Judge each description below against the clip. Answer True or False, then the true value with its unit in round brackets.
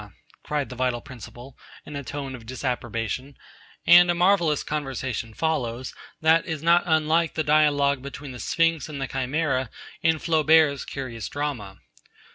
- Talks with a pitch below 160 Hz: True (140 Hz)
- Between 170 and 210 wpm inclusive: False (145 wpm)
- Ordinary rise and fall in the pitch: True (3.7 semitones)